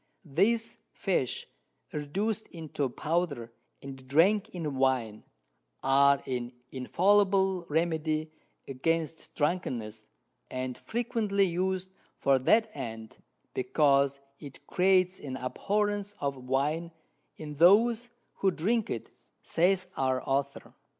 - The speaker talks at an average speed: No, slow, 105 wpm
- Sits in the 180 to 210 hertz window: No, medium, 155 Hz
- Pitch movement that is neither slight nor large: No, wide, 6.2 semitones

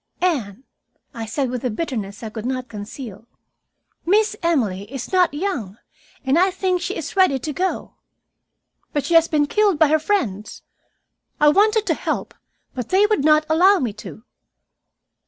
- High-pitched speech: Yes, very high, 295 Hz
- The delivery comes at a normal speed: Yes, average, 165 wpm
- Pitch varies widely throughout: Yes, wide, 7.9 semitones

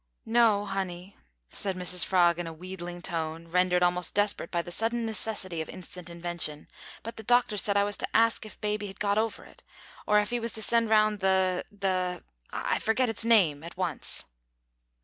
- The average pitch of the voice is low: No, high, 190 Hz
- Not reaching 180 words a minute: No, average, 190 wpm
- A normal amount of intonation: Yes, average, 3.5 semitones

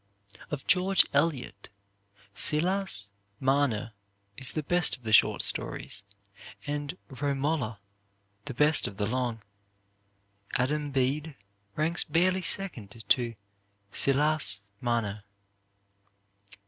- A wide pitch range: No, average, 4.9 semitones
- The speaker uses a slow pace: Yes, slow, 95 wpm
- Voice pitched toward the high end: No, medium, 140 Hz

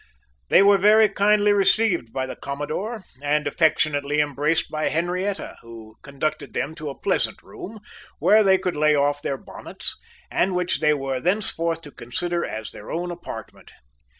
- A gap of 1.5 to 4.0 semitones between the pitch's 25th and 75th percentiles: No, average, 4.9 semitones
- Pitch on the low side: No, medium, 155 Hz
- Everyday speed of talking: Yes, average, 160 wpm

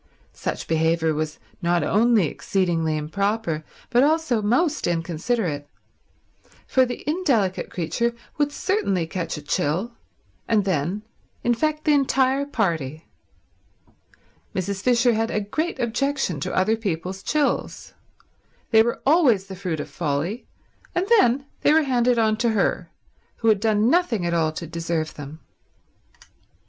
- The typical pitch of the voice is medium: No, high, 210 Hz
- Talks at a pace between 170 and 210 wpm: No, slow, 135 wpm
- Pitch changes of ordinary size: No, wide, 6.7 semitones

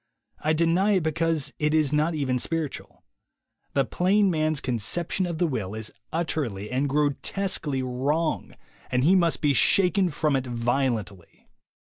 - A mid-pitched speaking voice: Yes, medium, 150 Hz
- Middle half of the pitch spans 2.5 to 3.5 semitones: No, average, 4.5 semitones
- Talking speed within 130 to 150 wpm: Yes, average, 145 wpm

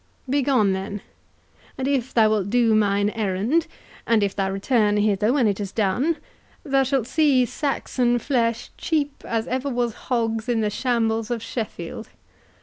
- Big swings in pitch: No, average, 3.8 semitones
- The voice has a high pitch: Yes, high, 230 Hz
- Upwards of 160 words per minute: No, average, 155 wpm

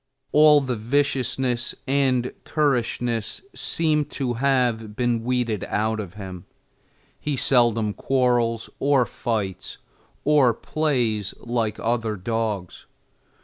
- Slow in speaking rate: Yes, slow, 105 wpm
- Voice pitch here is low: Yes, low, 120 Hz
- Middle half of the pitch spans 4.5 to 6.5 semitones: No, average, 3.4 semitones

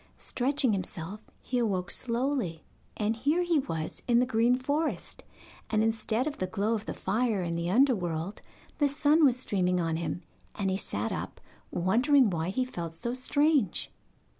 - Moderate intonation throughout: No, wide, 6.1 semitones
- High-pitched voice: Yes, high, 225 Hz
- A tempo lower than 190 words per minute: Yes, average, 165 wpm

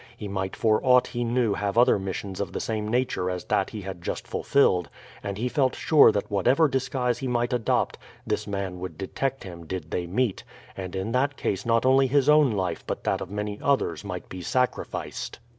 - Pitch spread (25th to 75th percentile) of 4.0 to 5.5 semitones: Yes, average, 5.0 semitones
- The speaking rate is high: Yes, fast, 210 wpm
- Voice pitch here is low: Yes, low, 110 Hz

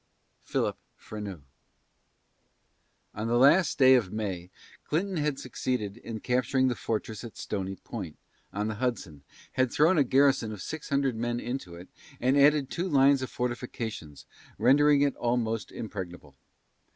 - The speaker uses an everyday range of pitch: Yes, average, 4.6 semitones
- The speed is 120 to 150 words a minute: Yes, average, 145 wpm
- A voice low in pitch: Yes, low, 120 Hz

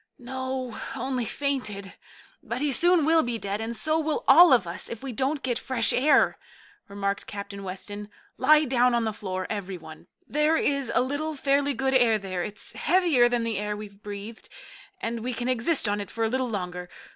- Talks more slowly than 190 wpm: No, average, 195 wpm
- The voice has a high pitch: Yes, high, 240 Hz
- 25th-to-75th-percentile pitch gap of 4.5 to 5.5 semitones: Yes, average, 4.8 semitones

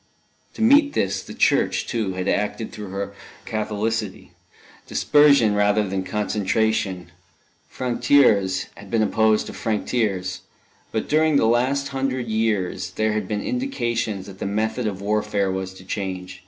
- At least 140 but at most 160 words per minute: Yes, average, 150 wpm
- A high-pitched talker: No, low, 105 Hz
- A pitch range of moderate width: Yes, average, 3.3 semitones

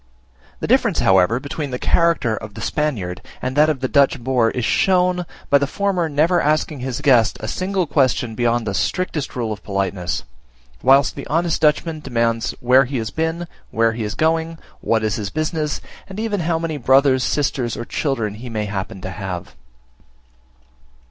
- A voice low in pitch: Yes, low, 130 Hz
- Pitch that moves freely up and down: Yes, wide, 5.7 semitones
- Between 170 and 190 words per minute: Yes, average, 180 wpm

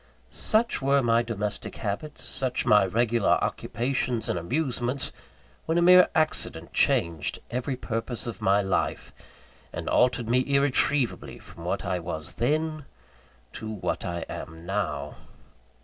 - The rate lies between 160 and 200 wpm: No, slow, 135 wpm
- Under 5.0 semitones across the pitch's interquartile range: No, wide, 5.5 semitones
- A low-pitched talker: Yes, low, 120 Hz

